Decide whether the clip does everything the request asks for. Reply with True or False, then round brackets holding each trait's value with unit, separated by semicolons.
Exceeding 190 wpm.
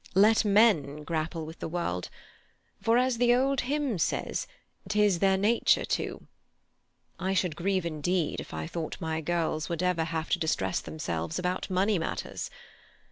False (155 wpm)